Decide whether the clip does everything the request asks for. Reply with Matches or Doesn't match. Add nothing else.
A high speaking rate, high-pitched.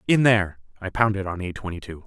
Doesn't match